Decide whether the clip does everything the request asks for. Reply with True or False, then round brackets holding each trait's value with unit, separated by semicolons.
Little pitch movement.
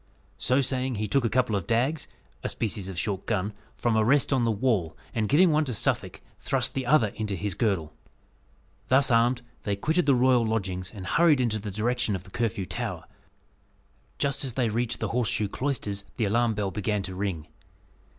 False (4.1 semitones)